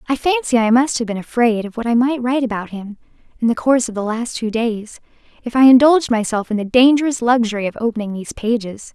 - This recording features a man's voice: No, female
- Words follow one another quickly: Yes, fast, 230 wpm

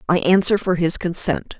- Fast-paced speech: No, average, 190 wpm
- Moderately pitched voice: Yes, medium, 175 Hz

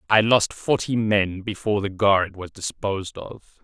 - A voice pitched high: No, low, 100 Hz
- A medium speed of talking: Yes, average, 165 wpm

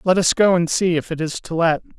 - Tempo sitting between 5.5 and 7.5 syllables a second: Yes, 5.7 syllables/s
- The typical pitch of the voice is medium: Yes, medium, 170 Hz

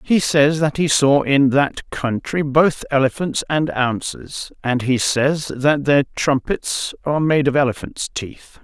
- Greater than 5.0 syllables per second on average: No, 3.9 syllables/s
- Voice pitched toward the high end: No, medium, 140 Hz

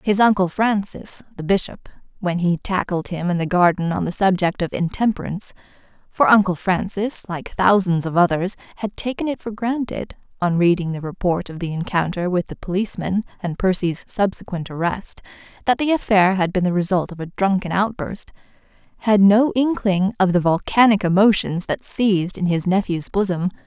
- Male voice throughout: No, female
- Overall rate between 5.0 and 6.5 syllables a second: Yes, 5.2 syllables/s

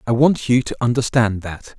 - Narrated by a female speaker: No, male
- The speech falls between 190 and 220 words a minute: Yes, average, 200 wpm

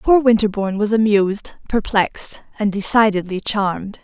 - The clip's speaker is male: No, female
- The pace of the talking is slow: Yes, slow, 120 wpm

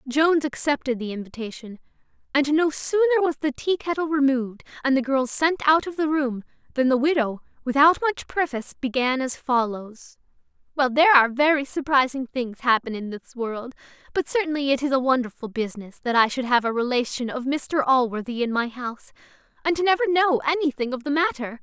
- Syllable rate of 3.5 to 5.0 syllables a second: No, 5.6 syllables/s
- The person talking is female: Yes, female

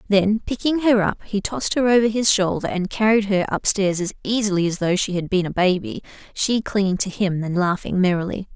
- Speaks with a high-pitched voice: Yes, high, 195 Hz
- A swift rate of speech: Yes, fast, 215 wpm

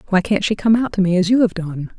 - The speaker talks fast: Yes, fast, 335 wpm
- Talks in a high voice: Yes, high, 195 Hz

